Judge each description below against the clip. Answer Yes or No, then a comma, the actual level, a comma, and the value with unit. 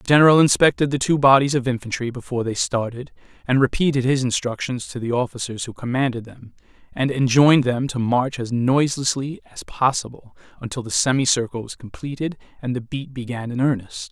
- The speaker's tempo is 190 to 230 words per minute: No, average, 175 wpm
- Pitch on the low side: Yes, low, 130 Hz